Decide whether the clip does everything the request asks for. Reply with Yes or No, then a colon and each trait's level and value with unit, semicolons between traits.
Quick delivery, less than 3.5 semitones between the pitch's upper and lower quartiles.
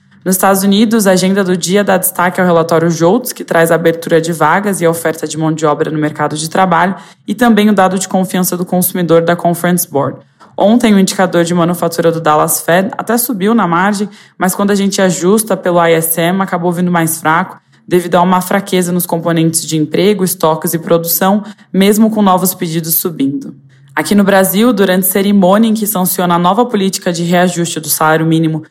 Yes: fast, 200 wpm; average, 2.8 semitones